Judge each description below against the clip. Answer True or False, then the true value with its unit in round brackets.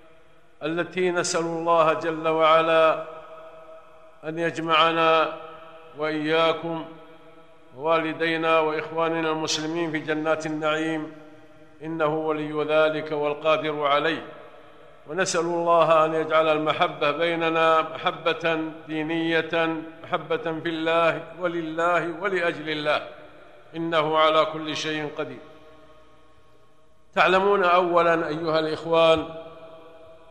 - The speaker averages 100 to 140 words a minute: False (85 wpm)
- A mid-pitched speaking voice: True (160 Hz)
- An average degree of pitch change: False (0.9 semitones)